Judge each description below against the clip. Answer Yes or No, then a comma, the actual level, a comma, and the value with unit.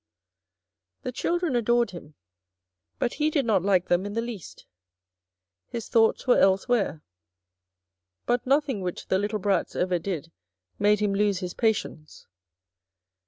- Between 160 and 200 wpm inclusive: No, slow, 135 wpm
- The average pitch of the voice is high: Yes, high, 205 Hz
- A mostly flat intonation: No, average, 4.5 semitones